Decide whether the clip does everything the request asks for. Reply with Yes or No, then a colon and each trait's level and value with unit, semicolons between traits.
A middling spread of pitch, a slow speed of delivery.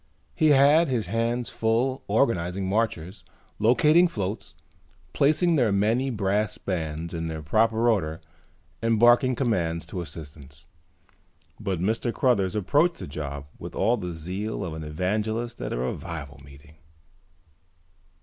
No: wide, 6.4 semitones; slow, 130 wpm